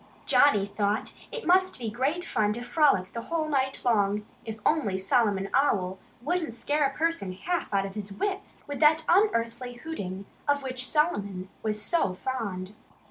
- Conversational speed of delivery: Yes, average, 165 wpm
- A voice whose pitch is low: No, high, 240 Hz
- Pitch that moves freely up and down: Yes, wide, 7.1 semitones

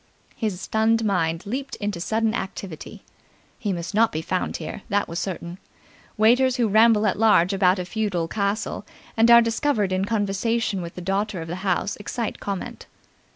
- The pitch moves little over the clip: No, average, 3.5 semitones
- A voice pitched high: Yes, high, 205 Hz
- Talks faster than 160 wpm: Yes, average, 170 wpm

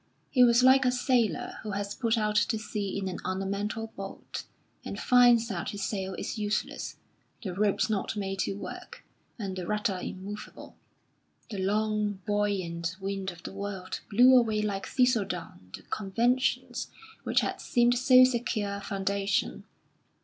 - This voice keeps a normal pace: Yes, average, 155 wpm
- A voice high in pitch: Yes, high, 205 Hz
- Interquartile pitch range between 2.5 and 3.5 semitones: Yes, average, 2.9 semitones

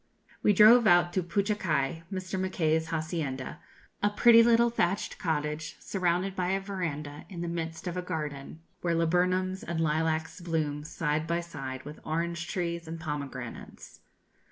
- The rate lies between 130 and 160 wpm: Yes, average, 150 wpm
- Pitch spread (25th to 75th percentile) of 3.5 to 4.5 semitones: No, average, 2.9 semitones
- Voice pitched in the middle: Yes, medium, 170 Hz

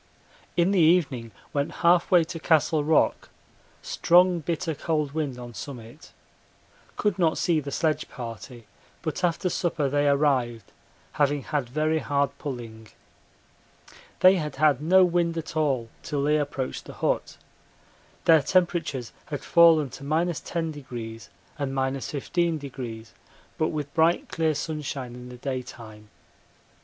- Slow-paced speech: Yes, slow, 130 wpm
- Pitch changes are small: No, average, 4.1 semitones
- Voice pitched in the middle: Yes, medium, 145 Hz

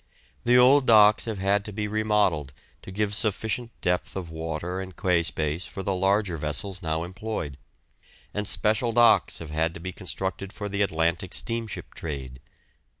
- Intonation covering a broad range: No, average, 4.4 semitones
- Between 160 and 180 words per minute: Yes, average, 165 wpm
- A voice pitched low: Yes, very low, 95 Hz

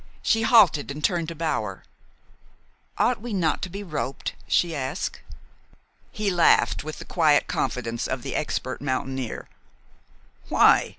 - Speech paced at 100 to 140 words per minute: Yes, slow, 135 wpm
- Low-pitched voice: No, medium, 155 Hz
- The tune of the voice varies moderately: No, wide, 5.7 semitones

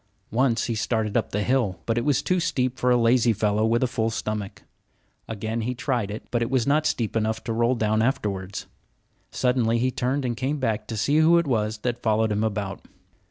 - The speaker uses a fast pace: Yes, fast, 215 wpm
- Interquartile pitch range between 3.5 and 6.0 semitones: No, average, 2.8 semitones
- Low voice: Yes, low, 115 Hz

